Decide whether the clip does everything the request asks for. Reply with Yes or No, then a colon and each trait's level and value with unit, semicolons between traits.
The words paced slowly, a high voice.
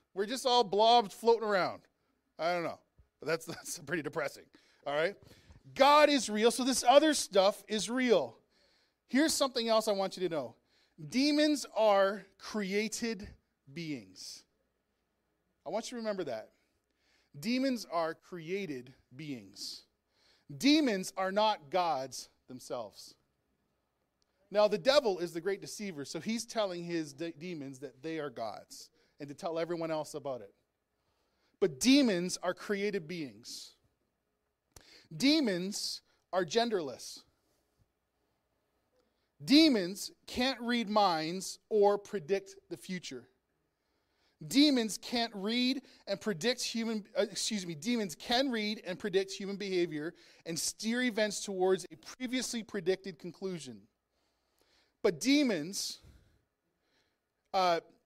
Yes: slow, 125 wpm; high, 200 Hz